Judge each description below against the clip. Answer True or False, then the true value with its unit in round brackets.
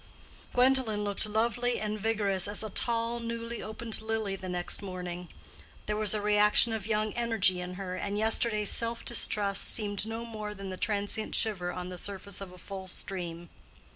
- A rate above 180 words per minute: False (175 wpm)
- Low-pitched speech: False (210 Hz)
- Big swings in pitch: False (2.7 semitones)